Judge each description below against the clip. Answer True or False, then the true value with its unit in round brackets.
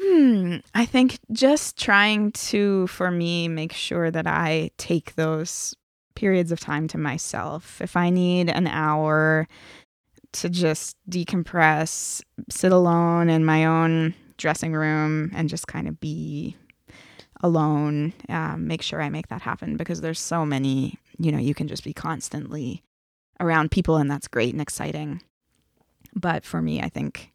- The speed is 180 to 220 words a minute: False (155 wpm)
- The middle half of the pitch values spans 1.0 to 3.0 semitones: True (2.6 semitones)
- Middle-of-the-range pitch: True (165 Hz)